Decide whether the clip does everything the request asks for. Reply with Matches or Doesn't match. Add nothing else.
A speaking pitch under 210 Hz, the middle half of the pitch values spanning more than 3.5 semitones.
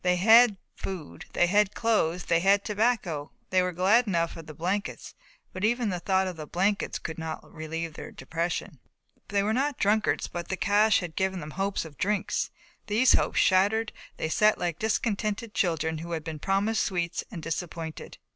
Matches